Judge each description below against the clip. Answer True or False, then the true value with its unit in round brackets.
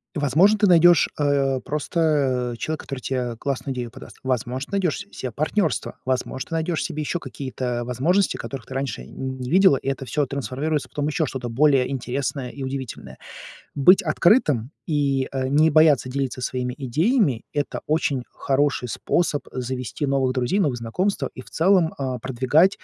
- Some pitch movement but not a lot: True (3.5 semitones)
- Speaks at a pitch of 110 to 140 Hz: True (135 Hz)